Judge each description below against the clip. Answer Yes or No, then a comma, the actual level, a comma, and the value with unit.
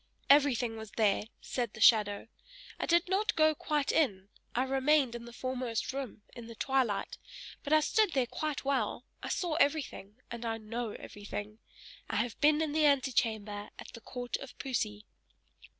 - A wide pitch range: No, average, 4.8 semitones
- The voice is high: Yes, high, 245 Hz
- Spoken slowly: No, average, 170 wpm